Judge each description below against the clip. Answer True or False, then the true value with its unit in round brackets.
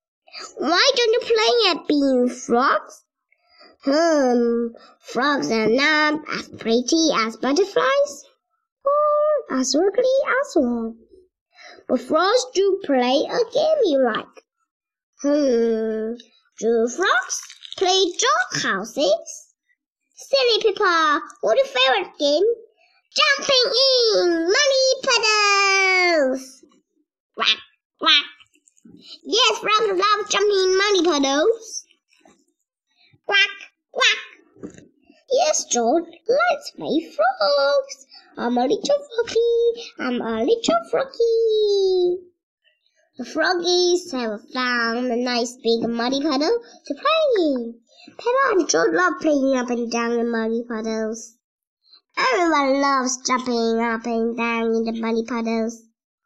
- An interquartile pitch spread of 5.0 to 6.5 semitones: False (7.8 semitones)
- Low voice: False (310 Hz)